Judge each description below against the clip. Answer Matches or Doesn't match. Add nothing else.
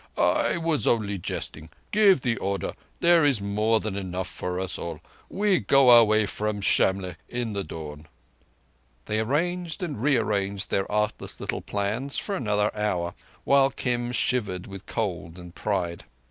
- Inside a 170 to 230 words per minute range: Doesn't match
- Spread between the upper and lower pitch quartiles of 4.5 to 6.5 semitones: Matches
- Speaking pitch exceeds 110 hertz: Doesn't match